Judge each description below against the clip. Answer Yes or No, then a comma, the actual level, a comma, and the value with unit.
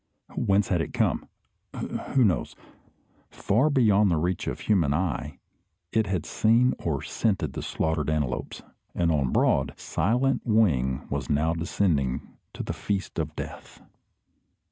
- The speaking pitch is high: No, very low, 85 Hz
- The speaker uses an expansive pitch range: Yes, wide, 6.0 semitones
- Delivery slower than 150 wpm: Yes, average, 140 wpm